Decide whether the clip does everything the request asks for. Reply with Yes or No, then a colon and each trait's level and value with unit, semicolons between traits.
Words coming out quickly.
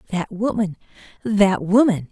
No: slow, 85 wpm